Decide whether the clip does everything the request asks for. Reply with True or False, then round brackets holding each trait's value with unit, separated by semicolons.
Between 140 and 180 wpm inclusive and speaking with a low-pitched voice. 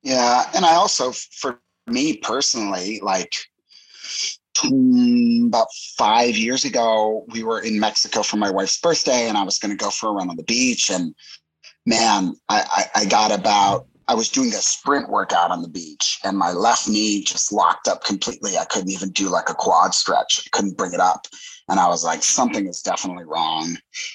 False (190 wpm; 120 Hz)